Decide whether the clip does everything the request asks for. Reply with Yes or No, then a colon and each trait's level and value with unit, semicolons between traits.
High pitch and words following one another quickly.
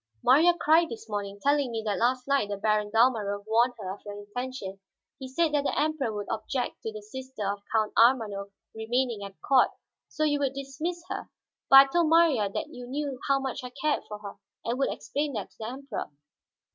Yes: high, 245 Hz; fast, 210 wpm